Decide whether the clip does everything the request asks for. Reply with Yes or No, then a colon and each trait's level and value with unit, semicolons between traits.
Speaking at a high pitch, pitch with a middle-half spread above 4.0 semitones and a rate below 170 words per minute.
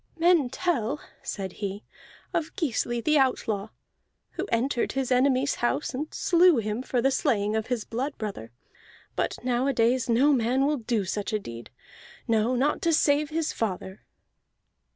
Yes: very high, 250 Hz; average, 4.6 semitones; average, 150 wpm